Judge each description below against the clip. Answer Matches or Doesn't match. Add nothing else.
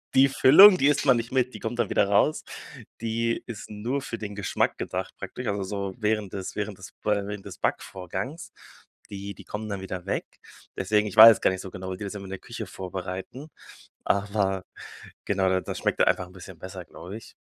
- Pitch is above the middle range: Doesn't match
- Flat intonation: Doesn't match